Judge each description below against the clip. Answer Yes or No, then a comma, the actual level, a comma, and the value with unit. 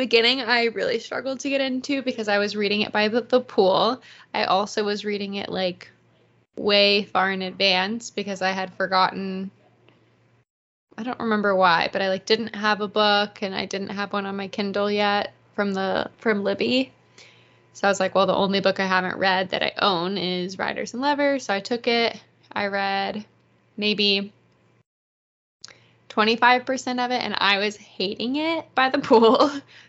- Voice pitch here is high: Yes, high, 205 Hz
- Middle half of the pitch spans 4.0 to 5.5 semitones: No, average, 3.2 semitones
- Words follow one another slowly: No, average, 180 wpm